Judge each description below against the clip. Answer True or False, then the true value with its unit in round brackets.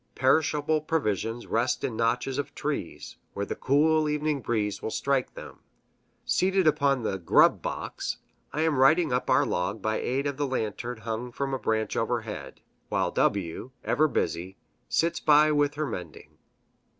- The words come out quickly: False (160 wpm)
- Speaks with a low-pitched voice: True (130 Hz)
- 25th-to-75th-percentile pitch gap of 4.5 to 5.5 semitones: True (5.1 semitones)